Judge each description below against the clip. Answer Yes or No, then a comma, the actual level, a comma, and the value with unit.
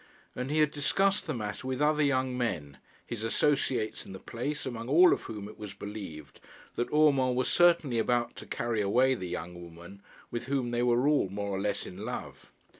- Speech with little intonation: No, average, 5.3 semitones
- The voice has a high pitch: No, low, 120 Hz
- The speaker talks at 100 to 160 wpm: No, average, 200 wpm